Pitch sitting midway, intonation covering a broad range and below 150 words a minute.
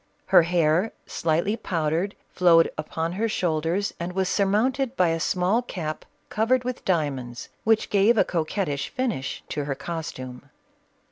No: medium, 175 Hz; average, 4.8 semitones; average, 140 wpm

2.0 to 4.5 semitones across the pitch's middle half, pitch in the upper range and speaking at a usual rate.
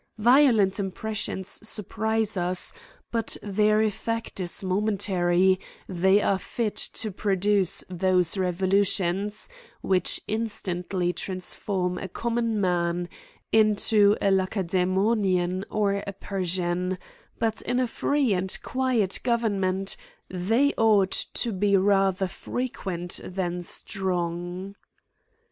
No: average, 2.8 semitones; high, 195 Hz; slow, 105 wpm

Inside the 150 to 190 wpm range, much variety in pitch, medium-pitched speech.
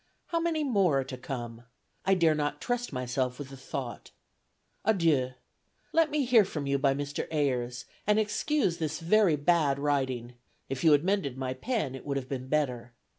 Yes: average, 180 wpm; wide, 6.6 semitones; medium, 145 Hz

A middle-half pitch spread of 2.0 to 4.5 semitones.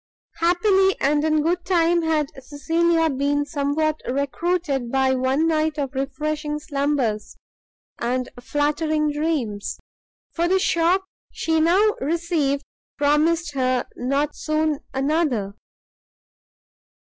Yes: average, 3.1 semitones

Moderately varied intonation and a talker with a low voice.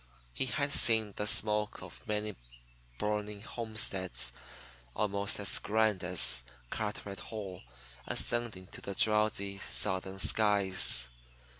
No: narrow, 2.1 semitones; low, 105 Hz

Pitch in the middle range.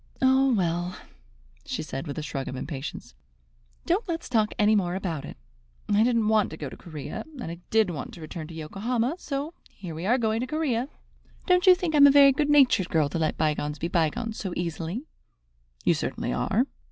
No: high, 205 Hz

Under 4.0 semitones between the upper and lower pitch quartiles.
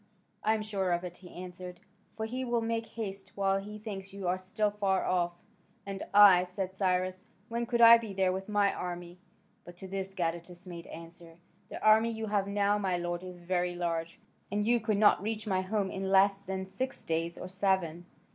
Yes: narrow, 2.6 semitones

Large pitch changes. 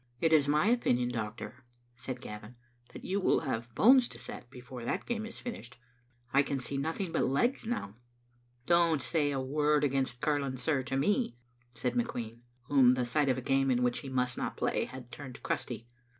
No: average, 3.7 semitones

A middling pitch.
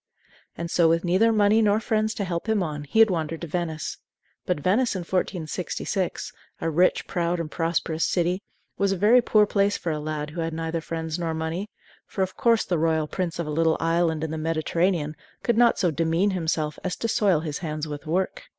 Yes: medium, 170 Hz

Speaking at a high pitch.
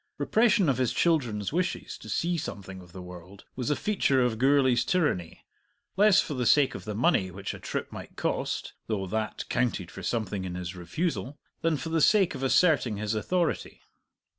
No: low, 125 Hz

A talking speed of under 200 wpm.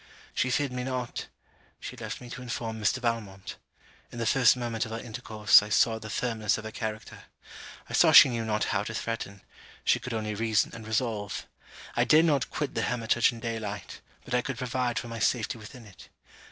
No: fast, 205 wpm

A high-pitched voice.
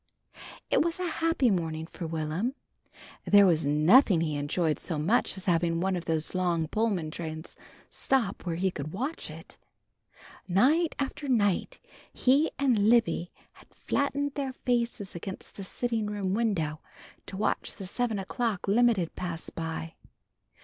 Yes: high, 195 Hz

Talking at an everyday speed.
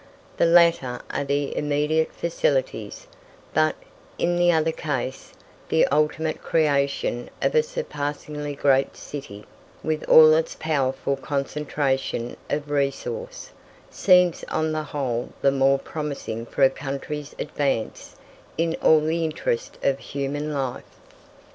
No: slow, 125 wpm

